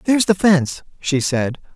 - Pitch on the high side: No, medium, 165 Hz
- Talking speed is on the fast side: No, average, 170 wpm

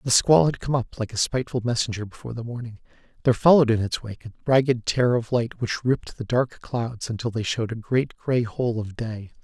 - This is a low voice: Yes, low, 120 Hz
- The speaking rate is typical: No, fast, 230 wpm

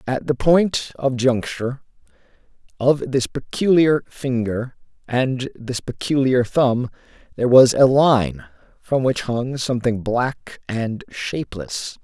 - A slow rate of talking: Yes, slow, 120 wpm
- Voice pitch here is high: No, low, 125 Hz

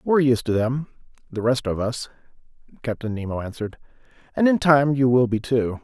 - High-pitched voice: No, low, 125 Hz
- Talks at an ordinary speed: Yes, average, 185 wpm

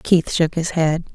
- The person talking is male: No, female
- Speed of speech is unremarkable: No, fast, 210 wpm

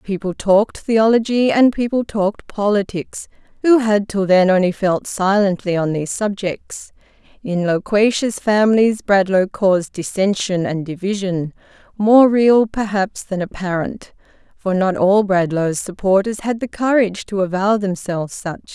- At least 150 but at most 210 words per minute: No, slow, 135 wpm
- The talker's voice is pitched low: No, high, 200 Hz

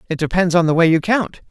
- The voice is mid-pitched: Yes, medium, 175 Hz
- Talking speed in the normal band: No, fast, 280 wpm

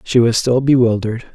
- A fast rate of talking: No, average, 180 wpm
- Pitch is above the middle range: No, low, 120 Hz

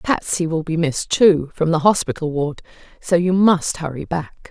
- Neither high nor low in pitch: Yes, medium, 165 Hz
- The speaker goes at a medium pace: Yes, average, 185 wpm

